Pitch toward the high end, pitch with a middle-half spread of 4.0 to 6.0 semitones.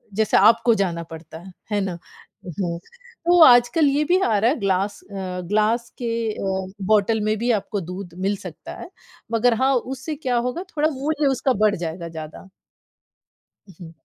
Yes: high, 215 Hz; average, 4.6 semitones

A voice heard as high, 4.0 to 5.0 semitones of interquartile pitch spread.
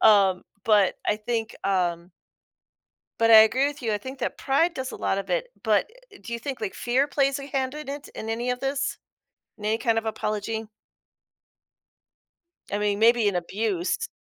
Yes: high, 225 Hz; average, 4.4 semitones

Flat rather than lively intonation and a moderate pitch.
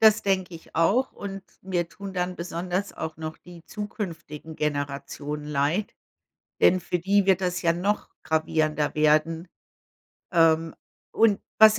No: average, 3.6 semitones; medium, 170 Hz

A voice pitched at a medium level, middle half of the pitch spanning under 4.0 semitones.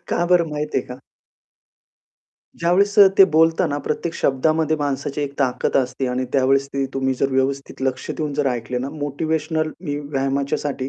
Yes: medium, 145 Hz; average, 2.8 semitones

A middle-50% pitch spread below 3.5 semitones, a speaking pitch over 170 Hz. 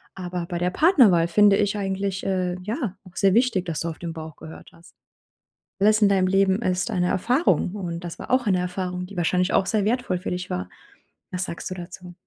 Yes: narrow, 2.4 semitones; medium, 185 Hz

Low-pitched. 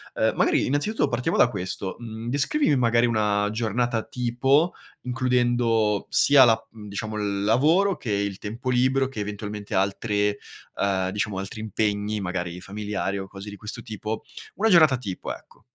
Yes: low, 110 Hz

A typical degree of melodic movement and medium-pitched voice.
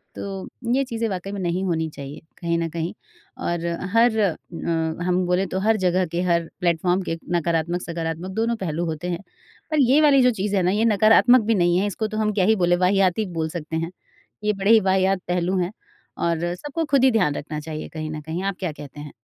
Yes: average, 3.8 semitones; medium, 180 Hz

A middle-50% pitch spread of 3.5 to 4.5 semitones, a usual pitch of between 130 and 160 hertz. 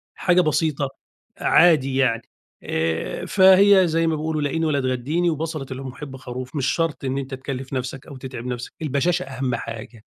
Yes: average, 3.9 semitones; low, 135 Hz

